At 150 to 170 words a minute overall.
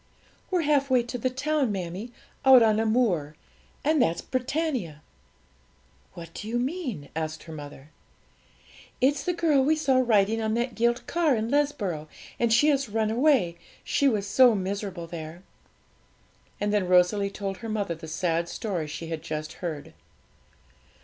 Yes: average, 160 wpm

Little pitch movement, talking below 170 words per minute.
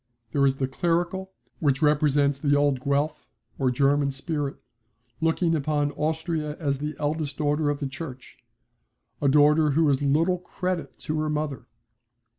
Yes: narrow, 2.2 semitones; average, 150 wpm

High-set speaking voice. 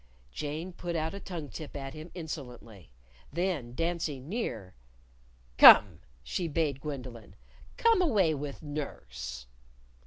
No: medium, 150 Hz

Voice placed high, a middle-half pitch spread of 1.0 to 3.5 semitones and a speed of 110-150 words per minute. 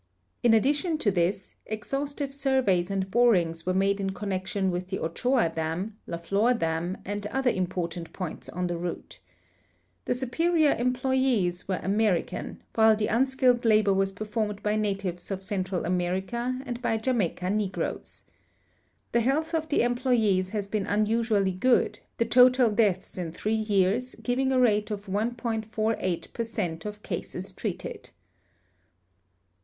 No: high, 210 Hz; average, 4.5 semitones; average, 145 wpm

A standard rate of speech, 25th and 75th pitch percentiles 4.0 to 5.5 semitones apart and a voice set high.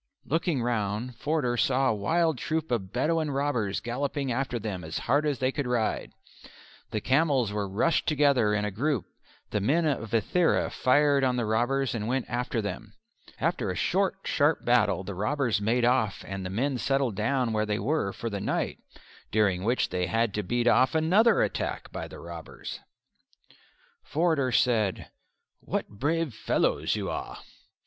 No: average, 170 wpm; average, 5.1 semitones; low, 125 Hz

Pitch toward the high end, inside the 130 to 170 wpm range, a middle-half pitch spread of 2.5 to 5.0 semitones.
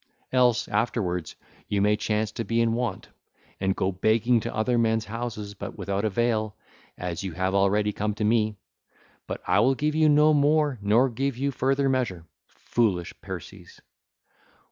No: low, 110 Hz; average, 165 wpm; average, 3.5 semitones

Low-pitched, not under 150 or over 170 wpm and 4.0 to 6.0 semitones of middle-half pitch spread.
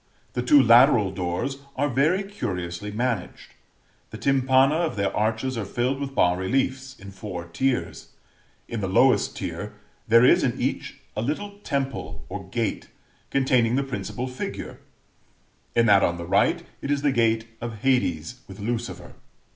Yes: low, 120 Hz; average, 155 wpm; average, 4.9 semitones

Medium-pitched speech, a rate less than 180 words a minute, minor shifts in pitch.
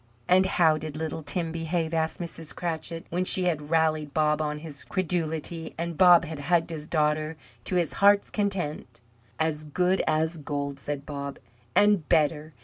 Yes: medium, 160 Hz; average, 165 wpm; narrow, 2.3 semitones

